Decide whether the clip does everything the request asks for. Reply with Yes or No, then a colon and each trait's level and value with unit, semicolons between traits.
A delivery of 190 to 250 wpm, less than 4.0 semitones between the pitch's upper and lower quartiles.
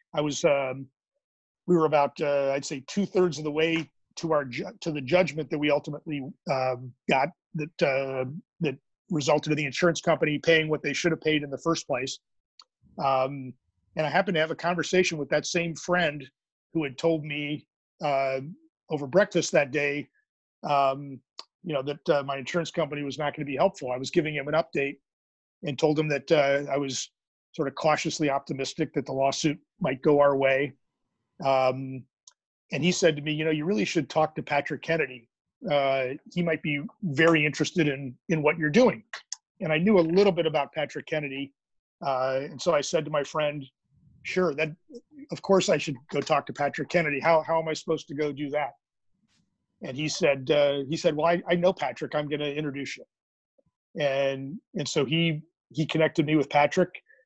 Yes: average, 200 wpm; average, 3.0 semitones